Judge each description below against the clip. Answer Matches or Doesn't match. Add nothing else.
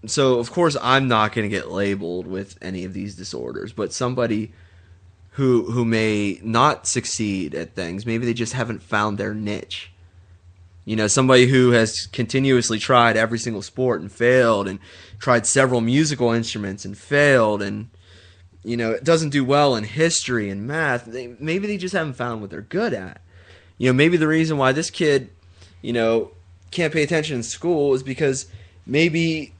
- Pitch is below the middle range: Matches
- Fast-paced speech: Doesn't match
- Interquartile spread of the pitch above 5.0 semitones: Matches